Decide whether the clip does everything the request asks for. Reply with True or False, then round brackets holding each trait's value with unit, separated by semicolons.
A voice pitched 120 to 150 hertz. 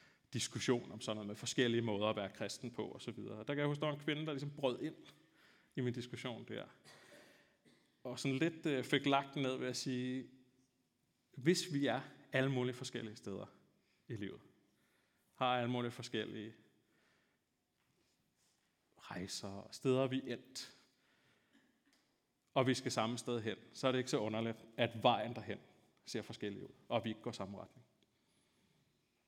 True (125 Hz)